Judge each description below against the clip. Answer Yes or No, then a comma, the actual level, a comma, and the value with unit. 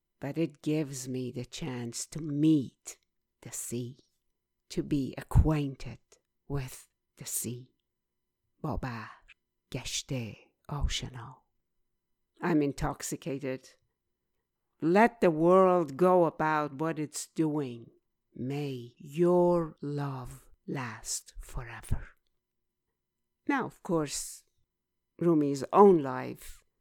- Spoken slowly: Yes, slow, 90 wpm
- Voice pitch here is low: No, medium, 145 Hz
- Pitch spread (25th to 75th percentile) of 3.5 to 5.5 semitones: Yes, average, 4.1 semitones